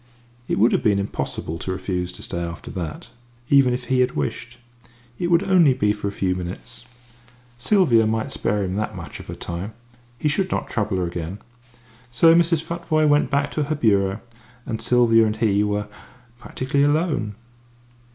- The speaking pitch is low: Yes, low, 115 Hz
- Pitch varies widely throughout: Yes, wide, 6.7 semitones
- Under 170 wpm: No, average, 180 wpm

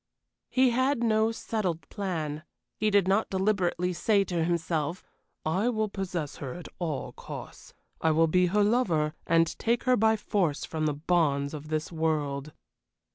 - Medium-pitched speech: Yes, medium, 175 Hz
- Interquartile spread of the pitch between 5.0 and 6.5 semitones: Yes, average, 5.3 semitones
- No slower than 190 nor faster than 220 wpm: No, average, 160 wpm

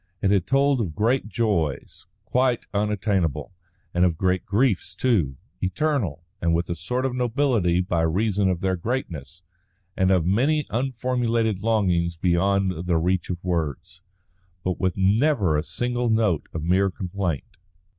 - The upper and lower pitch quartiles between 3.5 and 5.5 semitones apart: Yes, average, 5.0 semitones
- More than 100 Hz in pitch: No, very low, 95 Hz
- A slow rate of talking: No, average, 145 wpm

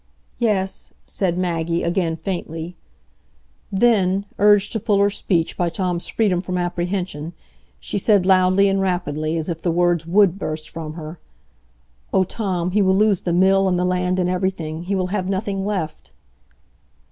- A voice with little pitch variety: Yes, narrow, 2.3 semitones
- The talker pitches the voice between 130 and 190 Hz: Yes, medium, 185 Hz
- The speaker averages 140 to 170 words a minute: Yes, average, 160 wpm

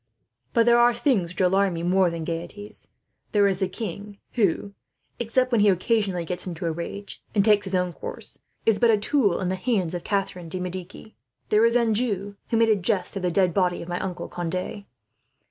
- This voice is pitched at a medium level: No, high, 195 Hz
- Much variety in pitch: No, average, 3.4 semitones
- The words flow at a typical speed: No, fast, 210 wpm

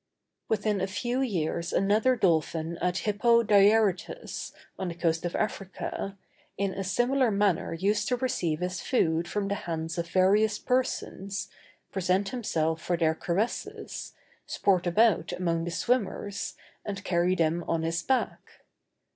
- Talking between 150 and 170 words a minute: No, average, 140 wpm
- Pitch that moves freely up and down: No, average, 3.9 semitones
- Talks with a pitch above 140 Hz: Yes, high, 190 Hz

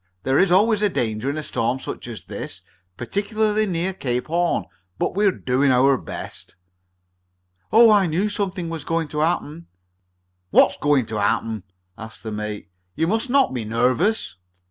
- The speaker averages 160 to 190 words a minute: Yes, average, 165 wpm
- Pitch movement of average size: No, wide, 8.4 semitones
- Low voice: No, medium, 155 Hz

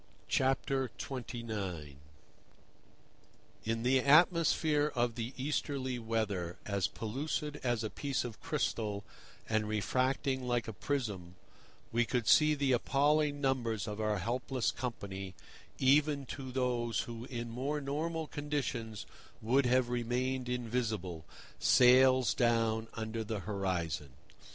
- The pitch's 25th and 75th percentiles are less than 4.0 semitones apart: Yes, average, 3.5 semitones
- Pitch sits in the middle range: No, low, 120 Hz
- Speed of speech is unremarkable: No, slow, 115 wpm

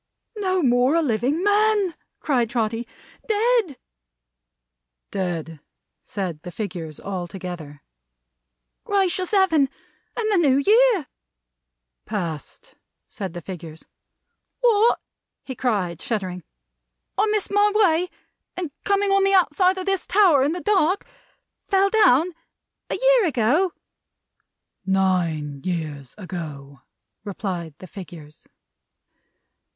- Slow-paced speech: Yes, slow, 110 wpm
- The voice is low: No, very high, 255 Hz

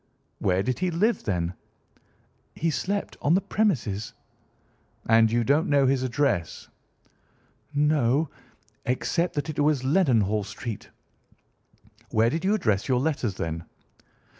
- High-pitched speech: No, low, 135 Hz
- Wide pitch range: Yes, wide, 6.5 semitones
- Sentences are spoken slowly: Yes, slow, 120 wpm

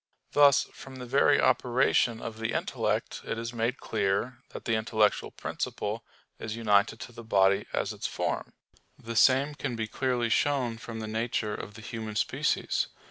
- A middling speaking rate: Yes, average, 170 wpm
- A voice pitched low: Yes, low, 115 Hz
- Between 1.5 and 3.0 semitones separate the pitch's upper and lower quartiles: Yes, narrow, 2.5 semitones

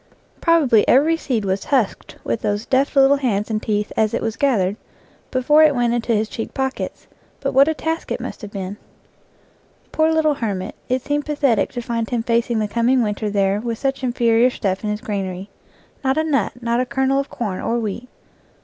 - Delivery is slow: No, average, 200 wpm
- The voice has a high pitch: Yes, high, 235 Hz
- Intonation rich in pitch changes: No, average, 4.4 semitones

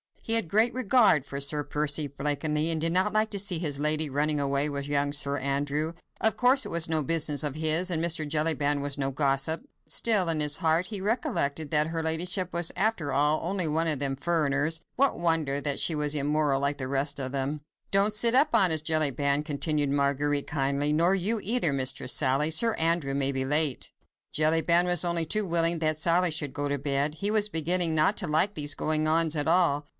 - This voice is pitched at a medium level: Yes, medium, 155 Hz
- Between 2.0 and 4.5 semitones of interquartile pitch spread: Yes, average, 3.2 semitones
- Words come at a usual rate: No, fast, 210 wpm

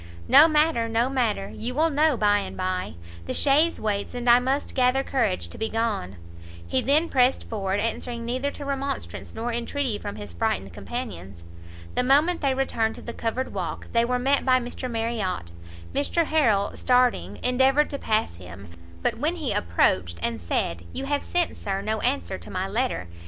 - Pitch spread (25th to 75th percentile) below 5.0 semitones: No, wide, 5.5 semitones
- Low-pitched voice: No, high, 240 Hz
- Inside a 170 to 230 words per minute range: Yes, average, 185 wpm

